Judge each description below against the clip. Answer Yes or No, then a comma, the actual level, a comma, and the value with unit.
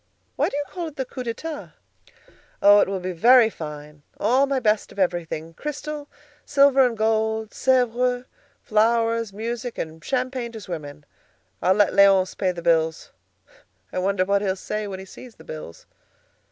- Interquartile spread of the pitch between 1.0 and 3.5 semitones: No, average, 5.2 semitones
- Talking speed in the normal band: Yes, average, 165 wpm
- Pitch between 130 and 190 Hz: No, high, 215 Hz